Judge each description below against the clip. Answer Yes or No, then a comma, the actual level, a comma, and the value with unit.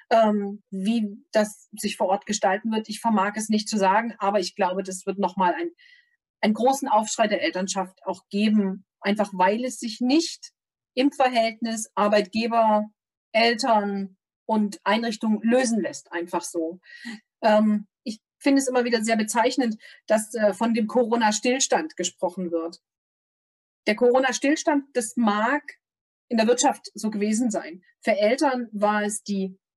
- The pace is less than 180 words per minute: Yes, average, 140 wpm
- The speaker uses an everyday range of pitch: Yes, average, 3.3 semitones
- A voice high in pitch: Yes, high, 215 Hz